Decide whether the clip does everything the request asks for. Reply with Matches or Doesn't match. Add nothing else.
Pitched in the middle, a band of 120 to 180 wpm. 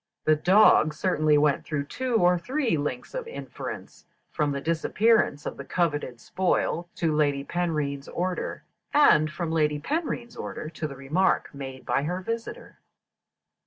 Matches